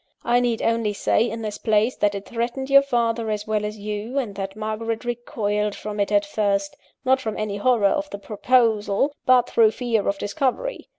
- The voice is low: No, high, 220 Hz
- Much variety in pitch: No, average, 2.7 semitones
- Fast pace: No, average, 195 wpm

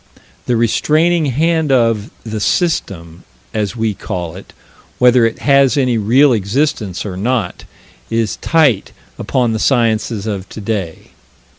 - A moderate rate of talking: No, slow, 130 wpm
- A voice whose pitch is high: No, low, 115 Hz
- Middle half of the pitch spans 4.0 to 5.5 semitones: Yes, average, 4.6 semitones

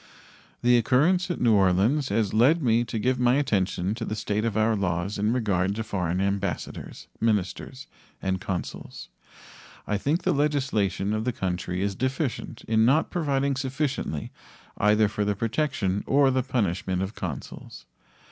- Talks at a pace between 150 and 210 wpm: Yes, average, 155 wpm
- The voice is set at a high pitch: No, low, 110 Hz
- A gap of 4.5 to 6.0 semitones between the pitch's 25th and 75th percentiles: Yes, average, 4.9 semitones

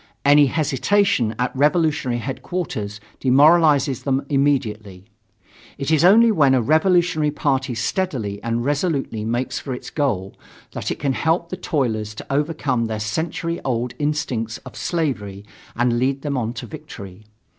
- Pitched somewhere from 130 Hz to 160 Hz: Yes, low, 135 Hz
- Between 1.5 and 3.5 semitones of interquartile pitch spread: No, average, 4.9 semitones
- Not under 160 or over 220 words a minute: No, average, 145 wpm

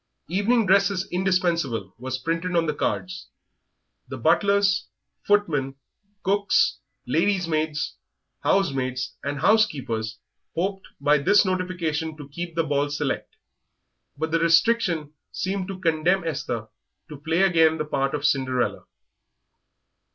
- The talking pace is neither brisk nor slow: No, slow, 120 wpm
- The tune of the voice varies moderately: Yes, average, 4.6 semitones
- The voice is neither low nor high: Yes, medium, 165 Hz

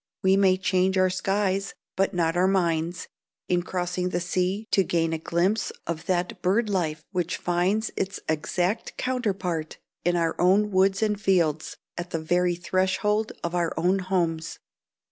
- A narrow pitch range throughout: Yes, narrow, 2.1 semitones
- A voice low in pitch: No, medium, 180 Hz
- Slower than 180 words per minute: Yes, average, 160 wpm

